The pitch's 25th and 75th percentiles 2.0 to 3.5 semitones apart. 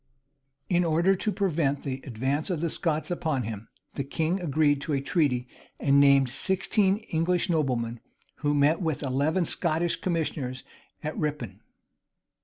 No: average, 4.0 semitones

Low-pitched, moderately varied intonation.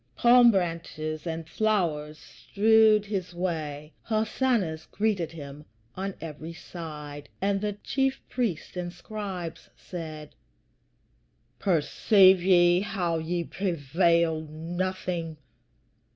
No: medium, 175 Hz; average, 4.0 semitones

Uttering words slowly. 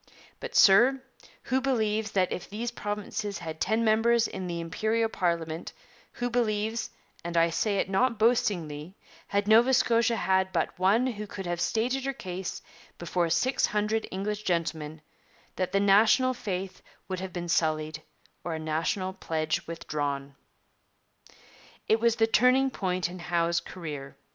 No: average, 150 wpm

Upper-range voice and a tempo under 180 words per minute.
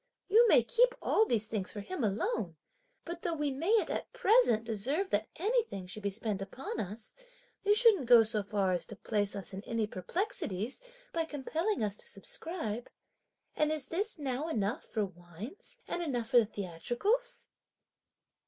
Yes: high, 240 Hz; average, 170 wpm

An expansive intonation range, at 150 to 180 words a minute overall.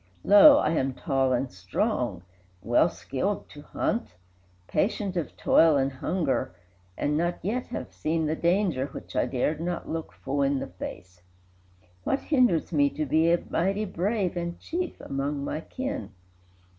Yes: wide, 5.7 semitones; average, 155 wpm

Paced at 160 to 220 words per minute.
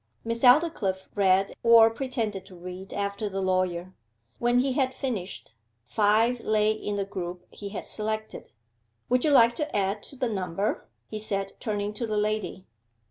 Yes: average, 165 wpm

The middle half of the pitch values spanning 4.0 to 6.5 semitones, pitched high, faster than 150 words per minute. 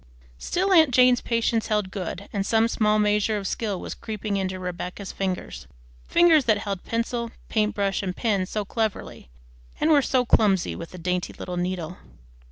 No: average, 3.6 semitones; high, 210 Hz; average, 175 wpm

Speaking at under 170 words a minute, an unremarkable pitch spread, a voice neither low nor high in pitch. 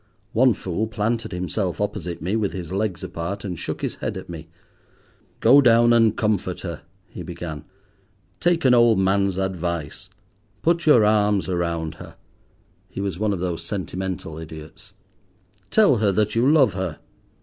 No: average, 160 wpm; average, 4.2 semitones; very low, 95 Hz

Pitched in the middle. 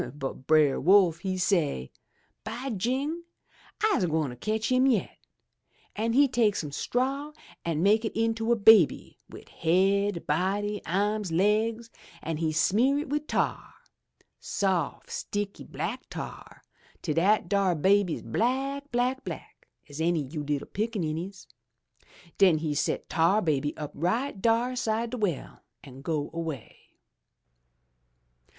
No: high, 200 Hz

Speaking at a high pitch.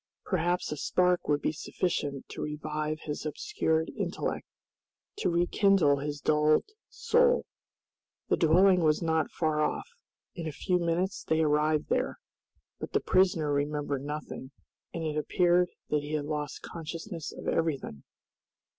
No: medium, 155 Hz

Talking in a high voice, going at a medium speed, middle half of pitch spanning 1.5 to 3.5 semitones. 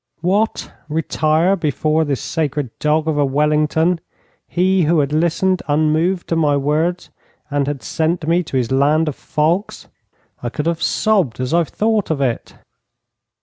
No: medium, 155 Hz; average, 155 wpm; average, 2.8 semitones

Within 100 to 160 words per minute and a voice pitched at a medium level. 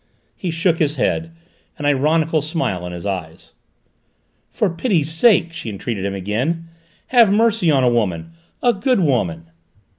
Yes: average, 150 wpm; medium, 150 Hz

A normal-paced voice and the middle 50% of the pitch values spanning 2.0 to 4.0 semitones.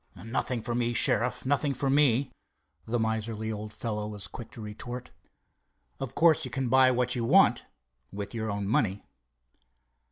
Yes: average, 155 wpm; average, 3.1 semitones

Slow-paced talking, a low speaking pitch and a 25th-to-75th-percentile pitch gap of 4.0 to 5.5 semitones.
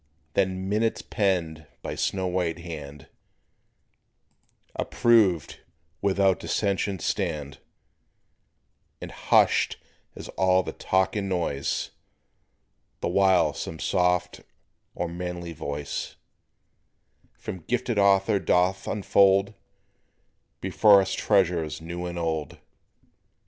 No: slow, 95 wpm; very low, 90 Hz; average, 2.8 semitones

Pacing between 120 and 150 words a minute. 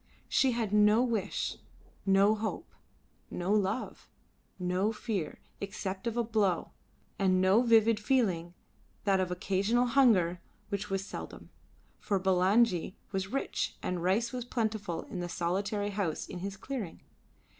Yes: average, 140 wpm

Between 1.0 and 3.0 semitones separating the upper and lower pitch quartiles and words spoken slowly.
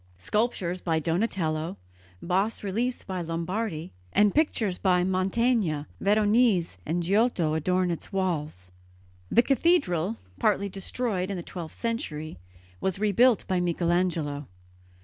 No: average, 4.3 semitones; slow, 115 wpm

